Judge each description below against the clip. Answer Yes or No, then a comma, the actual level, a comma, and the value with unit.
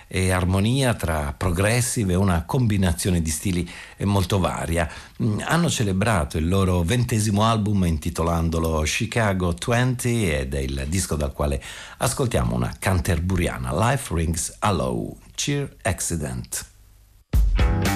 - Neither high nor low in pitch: No, very low, 95 Hz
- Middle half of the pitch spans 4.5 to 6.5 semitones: No, average, 4.0 semitones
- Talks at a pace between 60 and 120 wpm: Yes, slow, 115 wpm